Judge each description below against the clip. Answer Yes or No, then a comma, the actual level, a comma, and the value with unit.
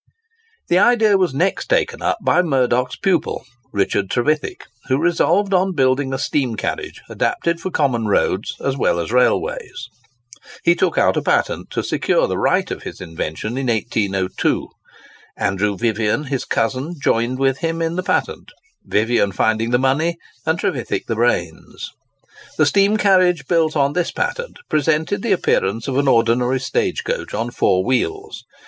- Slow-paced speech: No, average, 155 wpm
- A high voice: No, low, 135 Hz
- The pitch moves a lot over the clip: Yes, wide, 7.1 semitones